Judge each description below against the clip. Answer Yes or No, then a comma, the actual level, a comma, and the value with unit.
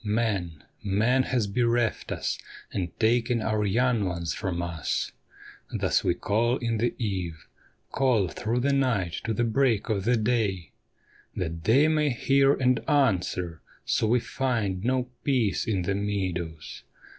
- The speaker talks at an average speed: Yes, average, 145 wpm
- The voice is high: No, low, 110 Hz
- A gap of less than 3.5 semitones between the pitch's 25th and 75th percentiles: No, average, 4.7 semitones